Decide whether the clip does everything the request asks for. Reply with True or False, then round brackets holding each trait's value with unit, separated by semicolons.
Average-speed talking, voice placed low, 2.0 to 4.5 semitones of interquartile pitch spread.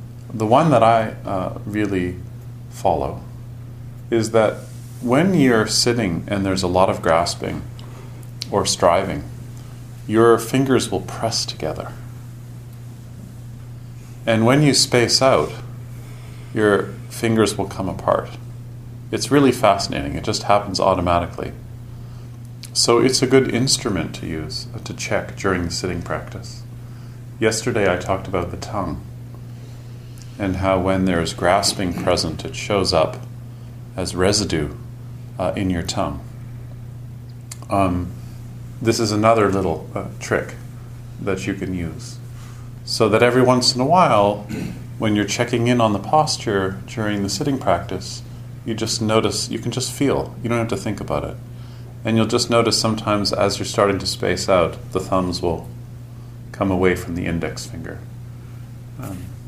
True (145 wpm; 120 Hz; 2.5 semitones)